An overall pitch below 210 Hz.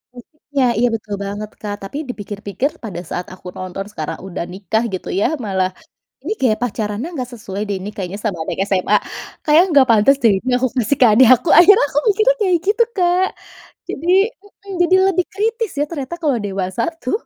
No: high, 235 Hz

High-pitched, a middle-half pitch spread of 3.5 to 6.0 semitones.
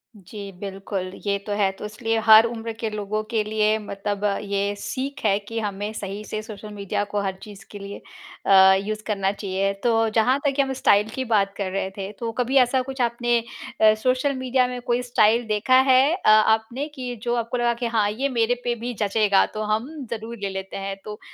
No: high, 215 Hz; average, 3.0 semitones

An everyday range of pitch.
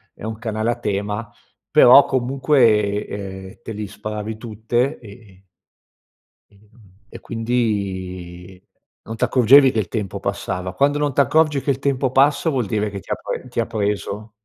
Yes: average, 4.0 semitones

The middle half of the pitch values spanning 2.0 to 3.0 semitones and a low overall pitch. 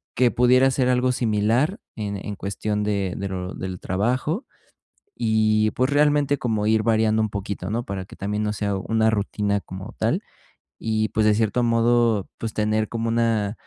Yes: narrow, 2.5 semitones; low, 110 Hz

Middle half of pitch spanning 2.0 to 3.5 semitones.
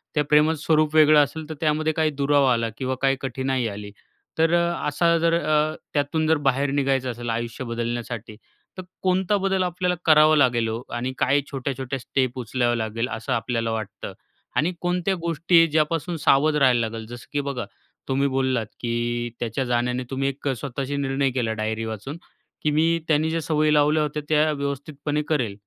No: average, 4.2 semitones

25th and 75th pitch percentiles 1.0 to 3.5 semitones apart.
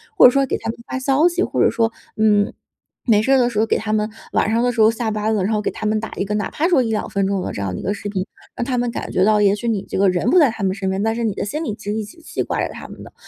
Yes: average, 2.9 semitones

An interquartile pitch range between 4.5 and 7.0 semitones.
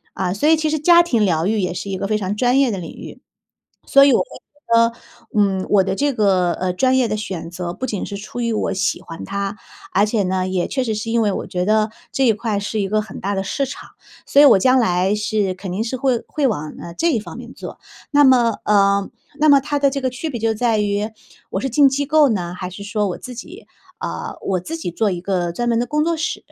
Yes: average, 5.2 semitones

